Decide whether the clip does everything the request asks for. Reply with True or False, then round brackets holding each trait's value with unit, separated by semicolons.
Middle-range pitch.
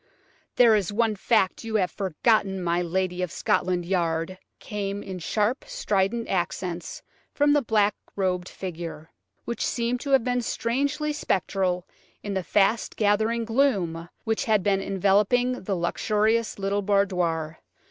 False (200 Hz)